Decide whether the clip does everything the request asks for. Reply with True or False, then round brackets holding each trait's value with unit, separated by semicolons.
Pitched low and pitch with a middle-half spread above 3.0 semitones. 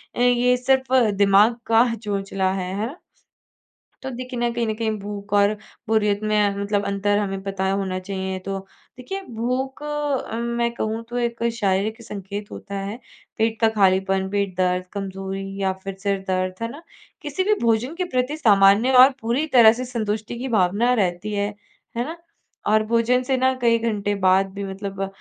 False (215 Hz; 3.5 semitones)